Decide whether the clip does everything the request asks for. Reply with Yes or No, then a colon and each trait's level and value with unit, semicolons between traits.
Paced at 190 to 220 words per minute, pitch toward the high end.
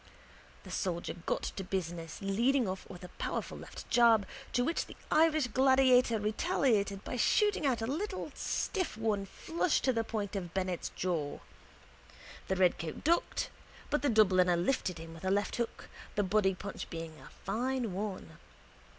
No: average, 160 wpm; high, 210 Hz